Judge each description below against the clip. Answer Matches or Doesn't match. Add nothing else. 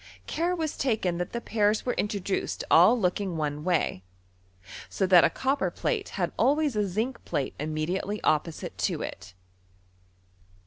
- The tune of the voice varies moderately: Doesn't match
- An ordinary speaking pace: Matches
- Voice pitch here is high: Matches